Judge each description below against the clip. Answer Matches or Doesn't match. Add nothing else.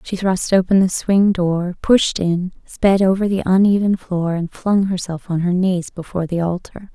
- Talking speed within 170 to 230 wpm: Matches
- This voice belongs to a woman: Matches